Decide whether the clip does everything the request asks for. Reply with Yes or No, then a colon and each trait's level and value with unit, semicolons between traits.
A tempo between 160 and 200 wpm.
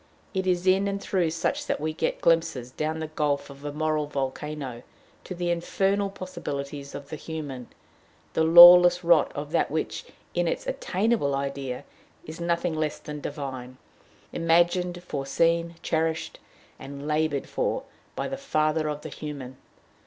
No: average, 150 wpm